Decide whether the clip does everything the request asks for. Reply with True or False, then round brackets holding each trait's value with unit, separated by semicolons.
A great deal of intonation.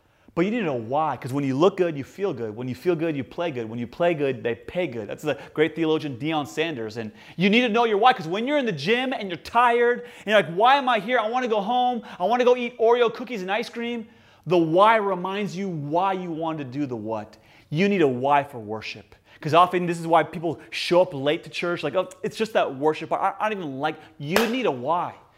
True (6.9 semitones)